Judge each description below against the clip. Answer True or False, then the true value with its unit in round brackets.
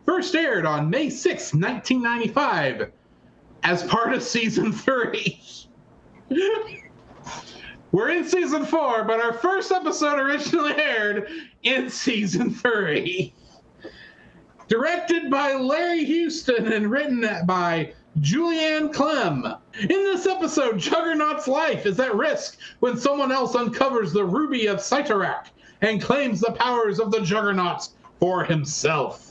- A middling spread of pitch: False (6.2 semitones)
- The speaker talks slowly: True (120 wpm)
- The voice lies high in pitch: True (260 Hz)